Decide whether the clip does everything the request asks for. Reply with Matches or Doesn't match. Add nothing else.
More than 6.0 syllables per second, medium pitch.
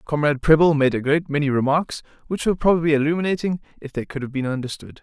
Matches